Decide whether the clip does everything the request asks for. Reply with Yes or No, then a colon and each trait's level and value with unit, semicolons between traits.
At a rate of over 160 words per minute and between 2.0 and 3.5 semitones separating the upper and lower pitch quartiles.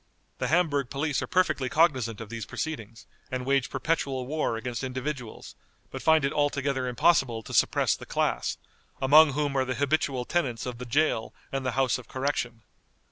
Yes: average, 175 wpm; average, 3.2 semitones